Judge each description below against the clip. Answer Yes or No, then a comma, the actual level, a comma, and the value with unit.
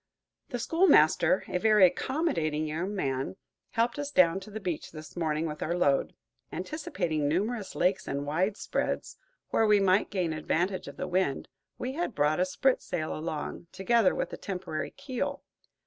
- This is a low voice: No, medium, 185 Hz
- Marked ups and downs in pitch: Yes, wide, 5.7 semitones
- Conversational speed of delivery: Yes, average, 165 wpm